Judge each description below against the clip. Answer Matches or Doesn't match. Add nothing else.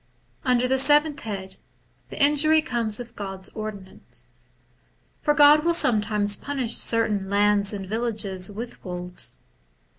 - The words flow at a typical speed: Doesn't match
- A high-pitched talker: Matches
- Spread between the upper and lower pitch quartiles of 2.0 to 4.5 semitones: Doesn't match